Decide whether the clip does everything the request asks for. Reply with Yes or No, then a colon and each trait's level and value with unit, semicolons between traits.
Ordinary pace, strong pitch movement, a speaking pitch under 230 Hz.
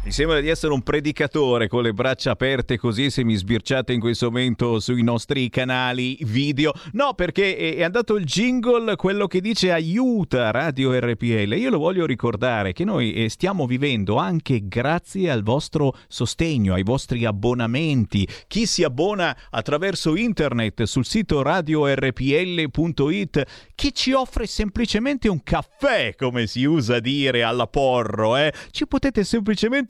Yes: average, 145 wpm; wide, 6.9 semitones; medium, 140 Hz